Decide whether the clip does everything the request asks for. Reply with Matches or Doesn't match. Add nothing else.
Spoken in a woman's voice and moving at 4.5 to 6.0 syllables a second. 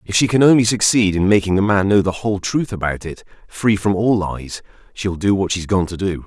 Doesn't match